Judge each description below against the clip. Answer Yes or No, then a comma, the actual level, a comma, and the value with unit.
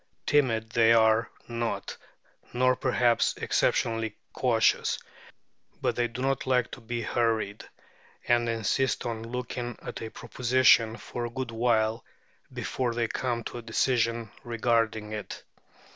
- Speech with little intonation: Yes, narrow, 1.5 semitones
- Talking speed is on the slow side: Yes, slow, 130 wpm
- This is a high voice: No, low, 115 Hz